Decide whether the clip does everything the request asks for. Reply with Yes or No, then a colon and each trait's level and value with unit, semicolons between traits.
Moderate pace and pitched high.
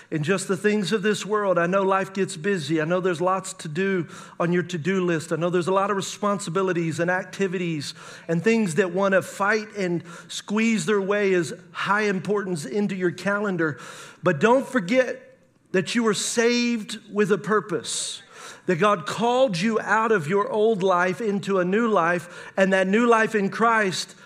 Yes: average, 190 wpm; high, 195 Hz